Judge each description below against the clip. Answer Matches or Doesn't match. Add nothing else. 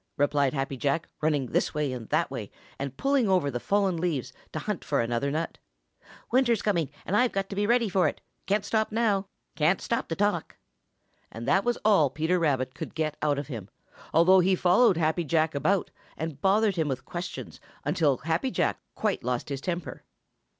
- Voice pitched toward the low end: Doesn't match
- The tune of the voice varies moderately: Doesn't match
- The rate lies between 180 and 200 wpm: Matches